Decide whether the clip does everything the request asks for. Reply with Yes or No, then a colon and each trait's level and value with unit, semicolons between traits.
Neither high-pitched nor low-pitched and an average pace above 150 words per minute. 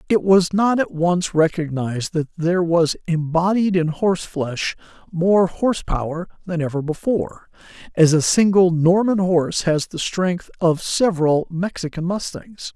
No: medium, 175 Hz; average, 145 wpm